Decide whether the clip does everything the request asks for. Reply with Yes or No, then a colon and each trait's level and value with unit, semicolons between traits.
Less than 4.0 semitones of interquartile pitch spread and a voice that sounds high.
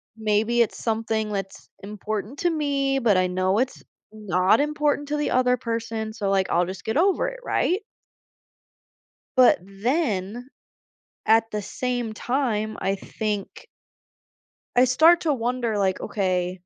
No: average, 4.5 semitones; high, 225 Hz